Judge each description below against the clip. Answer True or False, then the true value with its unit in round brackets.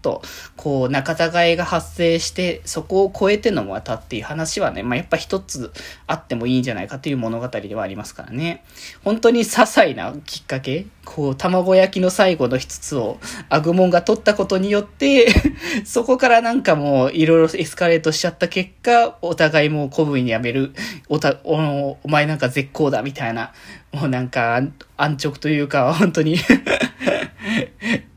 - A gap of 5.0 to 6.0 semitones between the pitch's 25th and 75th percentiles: True (5.3 semitones)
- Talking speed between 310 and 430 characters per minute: True (345 characters per minute)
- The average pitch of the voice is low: False (160 Hz)